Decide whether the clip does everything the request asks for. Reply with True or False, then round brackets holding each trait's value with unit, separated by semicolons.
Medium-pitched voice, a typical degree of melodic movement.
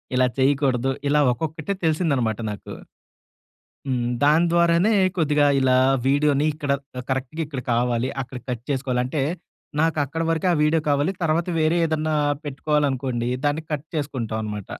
True (145 Hz; 3.6 semitones)